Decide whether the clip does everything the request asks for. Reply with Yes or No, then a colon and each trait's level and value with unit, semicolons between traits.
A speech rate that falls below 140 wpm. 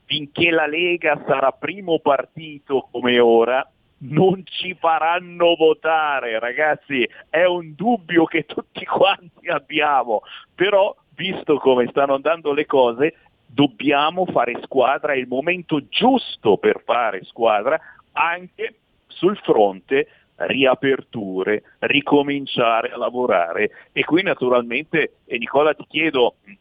Yes: slow, 115 wpm